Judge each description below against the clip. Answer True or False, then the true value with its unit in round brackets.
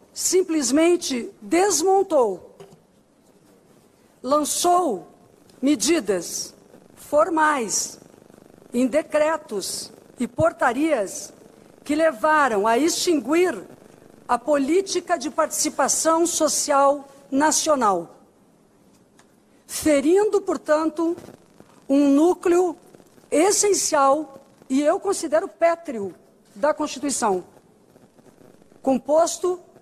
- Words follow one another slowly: True (60 wpm)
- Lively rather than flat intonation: False (3.4 semitones)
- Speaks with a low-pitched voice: False (305 Hz)